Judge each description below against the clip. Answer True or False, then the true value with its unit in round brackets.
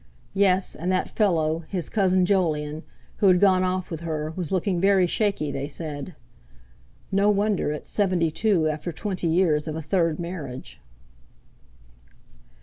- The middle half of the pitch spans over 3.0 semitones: True (3.6 semitones)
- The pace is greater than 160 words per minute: False (145 wpm)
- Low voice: False (175 Hz)